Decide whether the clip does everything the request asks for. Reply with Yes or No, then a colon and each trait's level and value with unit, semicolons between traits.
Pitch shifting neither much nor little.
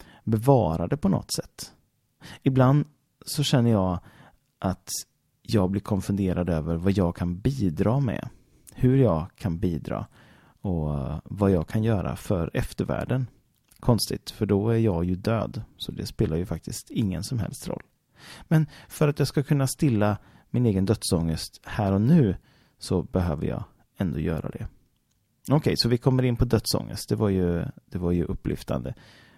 No: wide, 5.9 semitones